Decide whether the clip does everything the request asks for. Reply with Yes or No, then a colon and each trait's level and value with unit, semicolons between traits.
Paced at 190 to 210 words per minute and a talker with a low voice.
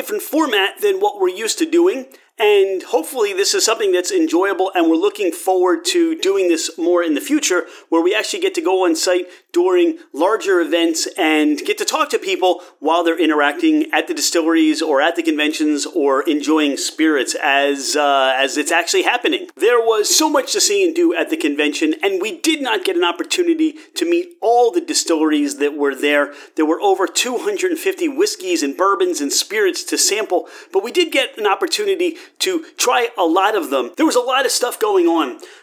No: fast, 205 wpm; very high, 335 Hz